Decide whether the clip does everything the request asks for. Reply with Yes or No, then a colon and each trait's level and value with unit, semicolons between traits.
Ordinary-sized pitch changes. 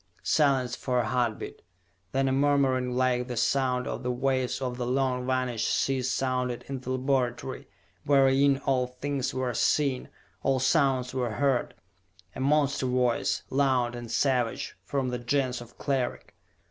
No: narrow, 1.5 semitones